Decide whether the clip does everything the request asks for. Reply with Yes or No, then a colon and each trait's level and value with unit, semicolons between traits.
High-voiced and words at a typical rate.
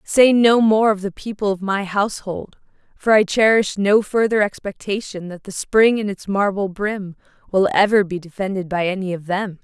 Yes: high, 200 Hz; average, 185 wpm